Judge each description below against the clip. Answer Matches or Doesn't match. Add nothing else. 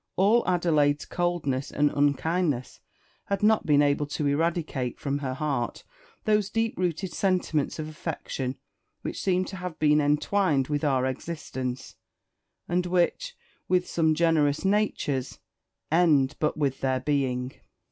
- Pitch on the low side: Doesn't match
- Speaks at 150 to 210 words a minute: Doesn't match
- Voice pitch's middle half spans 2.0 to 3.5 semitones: Doesn't match